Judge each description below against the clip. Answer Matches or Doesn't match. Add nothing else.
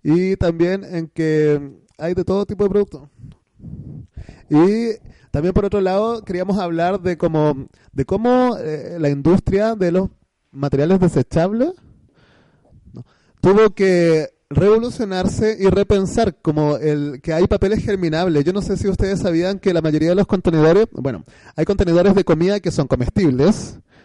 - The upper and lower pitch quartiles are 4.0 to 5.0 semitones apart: Matches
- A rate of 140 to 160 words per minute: Matches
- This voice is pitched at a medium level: Matches